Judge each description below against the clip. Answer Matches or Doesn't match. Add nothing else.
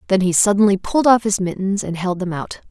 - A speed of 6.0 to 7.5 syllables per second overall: Matches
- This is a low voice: Doesn't match